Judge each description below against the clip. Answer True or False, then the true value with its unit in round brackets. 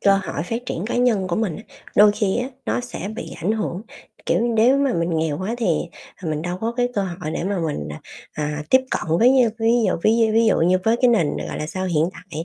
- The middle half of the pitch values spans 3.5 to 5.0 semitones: False (5.5 semitones)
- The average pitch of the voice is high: True (195 Hz)